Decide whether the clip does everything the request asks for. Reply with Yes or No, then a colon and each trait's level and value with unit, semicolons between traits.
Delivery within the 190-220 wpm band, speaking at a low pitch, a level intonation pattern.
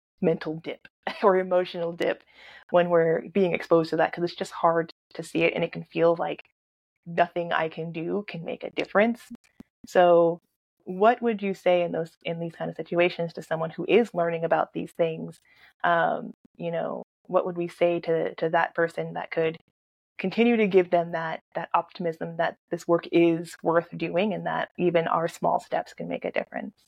No: average, 195 wpm; medium, 170 Hz; narrow, 1.5 semitones